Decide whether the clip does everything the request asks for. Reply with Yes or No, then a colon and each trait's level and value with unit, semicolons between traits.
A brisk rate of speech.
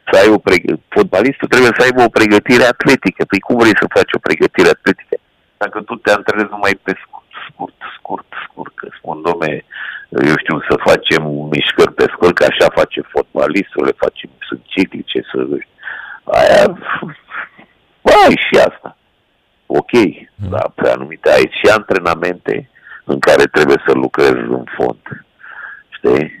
No: average, 150 wpm